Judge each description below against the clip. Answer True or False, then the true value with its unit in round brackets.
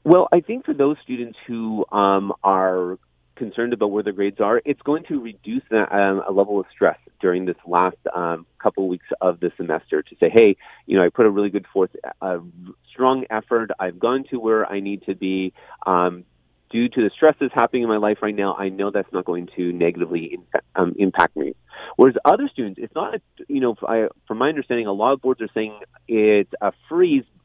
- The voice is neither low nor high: False (105 Hz)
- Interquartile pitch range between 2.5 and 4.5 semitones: False (5.3 semitones)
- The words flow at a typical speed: False (210 wpm)